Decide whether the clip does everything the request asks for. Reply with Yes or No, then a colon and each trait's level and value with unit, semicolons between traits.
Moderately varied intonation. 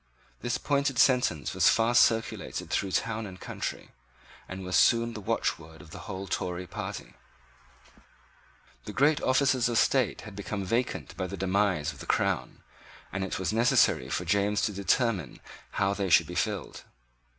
Yes: average, 4.2 semitones